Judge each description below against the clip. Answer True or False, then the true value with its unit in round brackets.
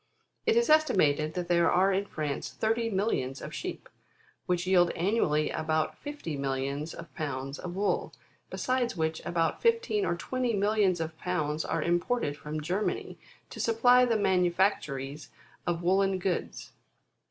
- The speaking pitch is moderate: True (175 Hz)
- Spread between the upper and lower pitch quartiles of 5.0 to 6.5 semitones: True (5.5 semitones)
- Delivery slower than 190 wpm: True (150 wpm)